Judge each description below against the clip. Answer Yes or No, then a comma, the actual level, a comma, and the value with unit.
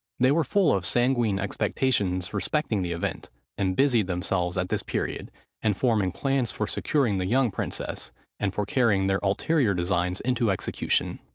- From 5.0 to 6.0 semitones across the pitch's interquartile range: Yes, wide, 5.4 semitones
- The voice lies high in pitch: No, low, 105 Hz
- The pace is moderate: Yes, average, 165 wpm